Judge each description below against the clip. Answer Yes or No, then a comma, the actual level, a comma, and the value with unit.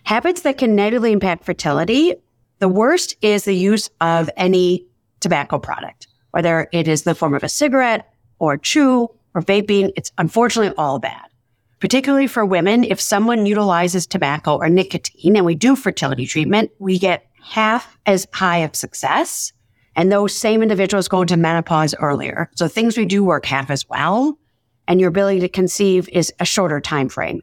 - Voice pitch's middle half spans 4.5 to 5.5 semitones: Yes, average, 4.9 semitones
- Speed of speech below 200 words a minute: Yes, average, 175 wpm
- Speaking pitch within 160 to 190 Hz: Yes, medium, 185 Hz